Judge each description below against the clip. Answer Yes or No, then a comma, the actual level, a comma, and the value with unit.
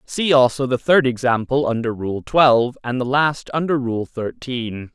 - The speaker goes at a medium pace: Yes, average, 170 wpm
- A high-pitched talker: No, low, 130 Hz